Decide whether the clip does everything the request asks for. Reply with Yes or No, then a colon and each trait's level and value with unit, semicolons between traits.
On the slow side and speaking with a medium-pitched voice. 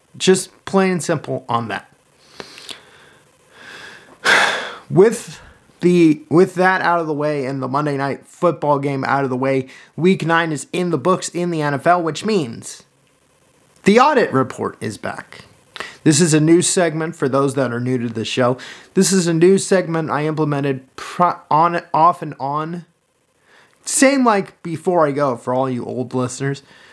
No: average, 165 wpm; medium, 155 Hz